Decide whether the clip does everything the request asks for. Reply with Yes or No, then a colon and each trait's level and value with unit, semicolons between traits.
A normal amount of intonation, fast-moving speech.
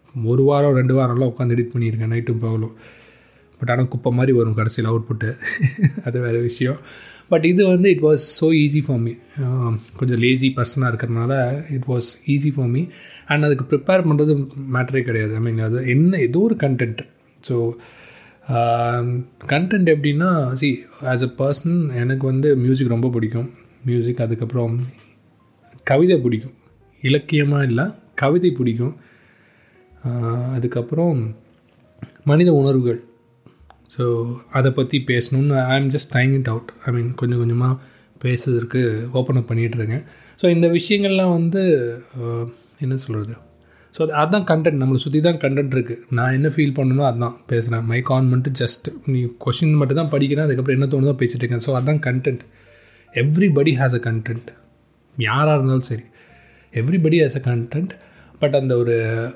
Yes: average, 3.3 semitones; fast, 140 wpm